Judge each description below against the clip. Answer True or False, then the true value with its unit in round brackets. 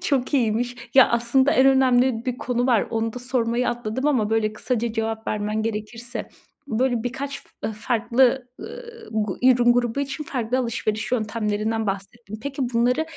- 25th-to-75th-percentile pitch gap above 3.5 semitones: False (2.7 semitones)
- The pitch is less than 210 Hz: False (240 Hz)